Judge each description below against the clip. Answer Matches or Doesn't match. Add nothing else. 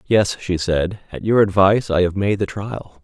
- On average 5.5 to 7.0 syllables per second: Doesn't match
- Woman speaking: Doesn't match